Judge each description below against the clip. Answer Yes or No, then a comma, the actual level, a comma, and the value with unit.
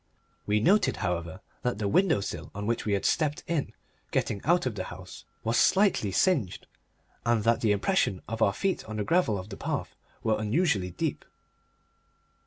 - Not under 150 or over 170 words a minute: No, average, 180 wpm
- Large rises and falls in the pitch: Yes, wide, 7.6 semitones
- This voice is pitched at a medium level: No, low, 110 Hz